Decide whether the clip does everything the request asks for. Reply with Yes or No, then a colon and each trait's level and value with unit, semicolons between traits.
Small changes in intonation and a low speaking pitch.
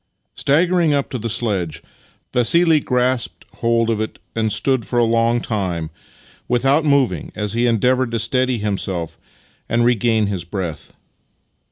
No: average, 3.6 semitones; low, 115 Hz